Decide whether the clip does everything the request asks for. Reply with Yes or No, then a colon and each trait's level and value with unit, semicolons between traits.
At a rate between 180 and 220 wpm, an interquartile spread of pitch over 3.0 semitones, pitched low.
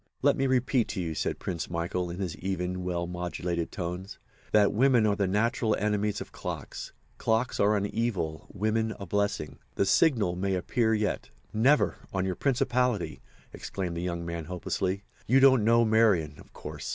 No: average, 170 wpm; average, 4.0 semitones; low, 100 Hz